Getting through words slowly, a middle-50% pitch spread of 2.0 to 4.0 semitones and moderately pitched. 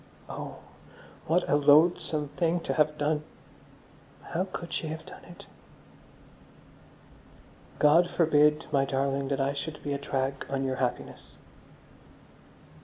Yes: slow, 125 wpm; average, 2.7 semitones; medium, 150 Hz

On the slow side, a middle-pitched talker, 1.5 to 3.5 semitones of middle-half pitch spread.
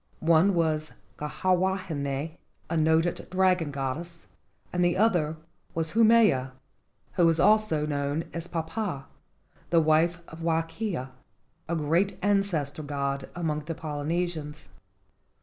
Yes: slow, 115 wpm; medium, 165 Hz; average, 3.1 semitones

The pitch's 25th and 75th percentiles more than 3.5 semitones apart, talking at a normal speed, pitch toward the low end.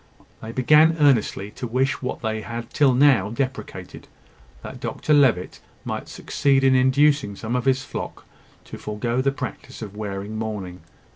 Yes: average, 3.9 semitones; average, 155 wpm; low, 125 Hz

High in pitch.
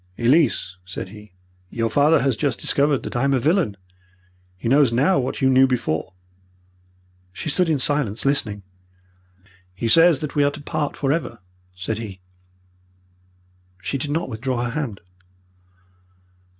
No: low, 135 Hz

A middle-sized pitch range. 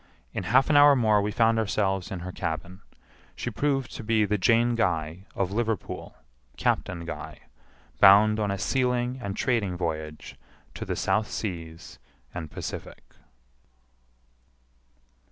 Yes: average, 4.4 semitones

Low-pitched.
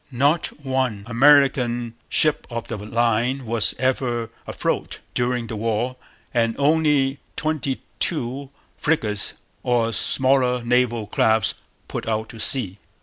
Yes: low, 125 Hz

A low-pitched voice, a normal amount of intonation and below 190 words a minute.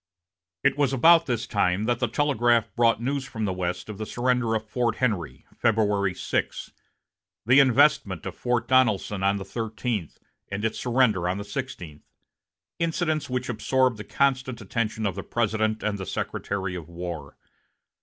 Yes: low, 110 Hz; average, 4.2 semitones; average, 165 wpm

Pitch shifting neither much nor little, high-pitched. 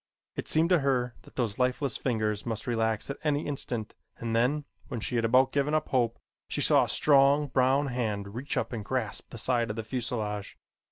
No: average, 3.6 semitones; low, 125 Hz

